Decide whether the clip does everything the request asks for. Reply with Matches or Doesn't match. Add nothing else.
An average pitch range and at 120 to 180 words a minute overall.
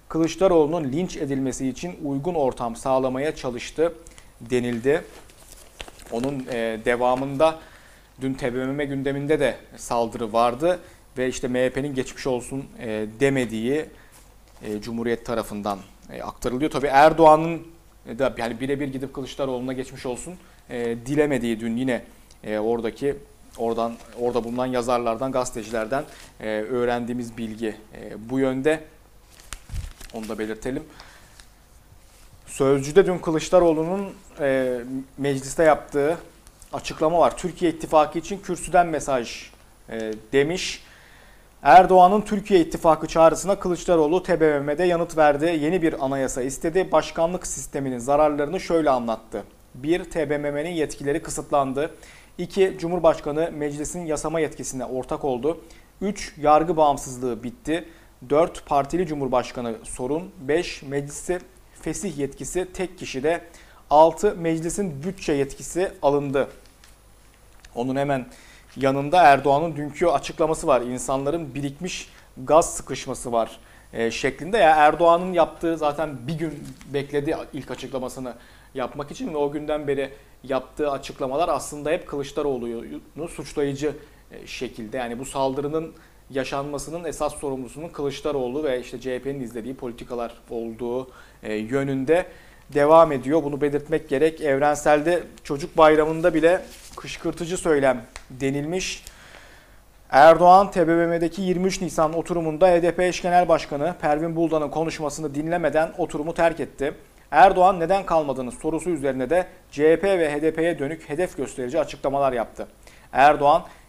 Doesn't match